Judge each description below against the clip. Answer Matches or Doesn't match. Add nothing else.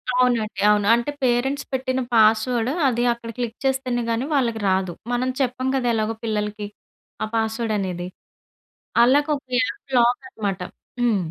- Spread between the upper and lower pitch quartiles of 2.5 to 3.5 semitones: Matches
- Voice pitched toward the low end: Doesn't match